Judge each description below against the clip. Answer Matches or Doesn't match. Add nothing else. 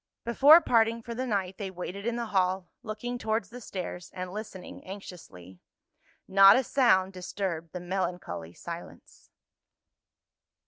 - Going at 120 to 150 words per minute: Matches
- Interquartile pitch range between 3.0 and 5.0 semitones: Matches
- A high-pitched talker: Matches